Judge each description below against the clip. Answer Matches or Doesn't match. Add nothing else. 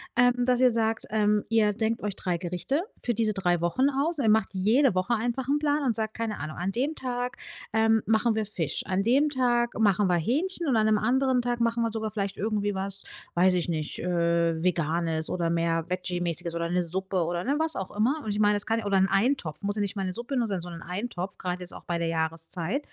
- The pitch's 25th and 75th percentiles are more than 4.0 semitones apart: Matches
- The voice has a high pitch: Matches